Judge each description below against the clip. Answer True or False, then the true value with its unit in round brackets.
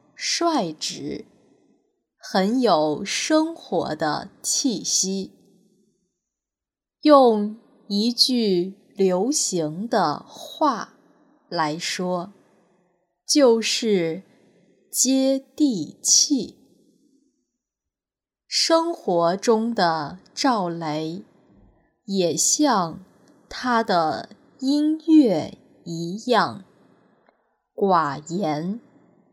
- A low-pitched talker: False (205 Hz)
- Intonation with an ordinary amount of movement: False (7.0 semitones)